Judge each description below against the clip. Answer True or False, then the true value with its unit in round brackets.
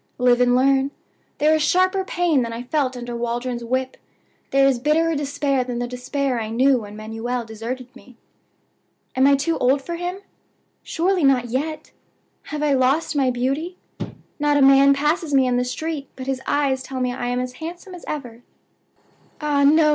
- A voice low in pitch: False (270 Hz)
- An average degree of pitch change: True (3.3 semitones)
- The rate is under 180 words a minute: False (185 wpm)